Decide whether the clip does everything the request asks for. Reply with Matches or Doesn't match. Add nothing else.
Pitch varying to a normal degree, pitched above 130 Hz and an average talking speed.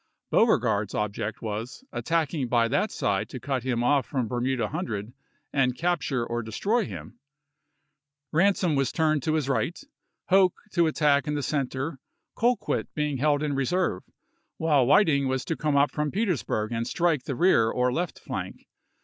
Matches